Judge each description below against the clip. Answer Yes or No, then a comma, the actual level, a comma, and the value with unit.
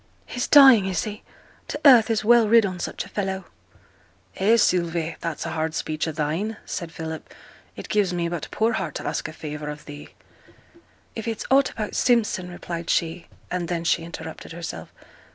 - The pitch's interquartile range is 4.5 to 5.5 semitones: Yes, average, 5.0 semitones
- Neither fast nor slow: Yes, average, 185 wpm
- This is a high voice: No, medium, 180 Hz